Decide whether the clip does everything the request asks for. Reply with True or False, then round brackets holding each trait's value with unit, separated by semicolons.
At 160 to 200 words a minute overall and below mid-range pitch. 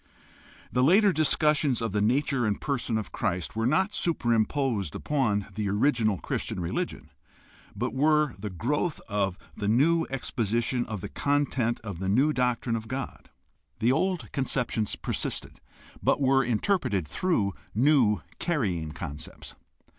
False (140 wpm; 120 Hz)